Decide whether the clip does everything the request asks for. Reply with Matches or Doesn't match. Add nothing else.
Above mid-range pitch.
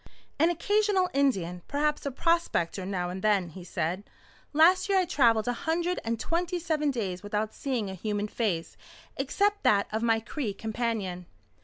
Matches